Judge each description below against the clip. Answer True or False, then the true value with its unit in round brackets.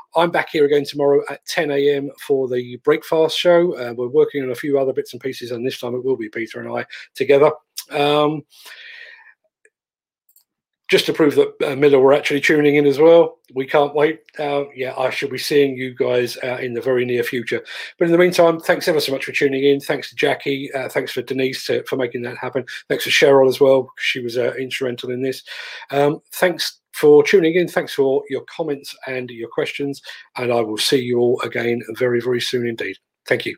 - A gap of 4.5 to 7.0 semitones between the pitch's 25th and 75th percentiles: False (3.3 semitones)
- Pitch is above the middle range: False (140 Hz)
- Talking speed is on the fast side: True (220 wpm)